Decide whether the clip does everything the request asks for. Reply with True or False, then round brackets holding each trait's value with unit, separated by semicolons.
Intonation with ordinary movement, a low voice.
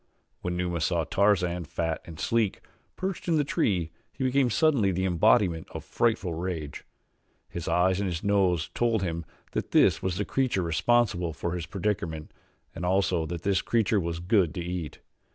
True (3.7 semitones; 90 Hz)